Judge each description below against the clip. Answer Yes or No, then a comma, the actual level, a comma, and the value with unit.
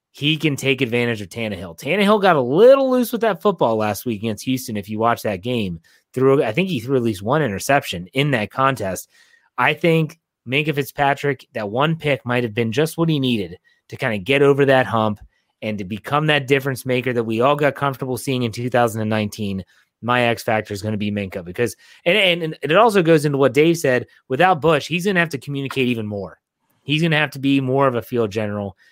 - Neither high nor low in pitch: No, low, 130 Hz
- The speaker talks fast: Yes, fast, 230 wpm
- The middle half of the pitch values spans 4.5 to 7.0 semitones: Yes, average, 4.9 semitones